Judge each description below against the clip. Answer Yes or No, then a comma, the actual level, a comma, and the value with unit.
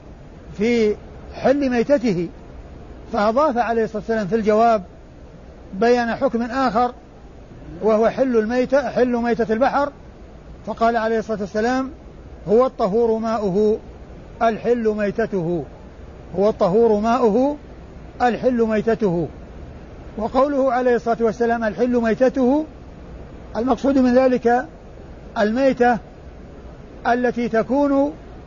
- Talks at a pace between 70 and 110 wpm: Yes, average, 95 wpm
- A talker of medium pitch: No, high, 230 Hz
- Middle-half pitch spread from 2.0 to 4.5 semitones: Yes, narrow, 2.4 semitones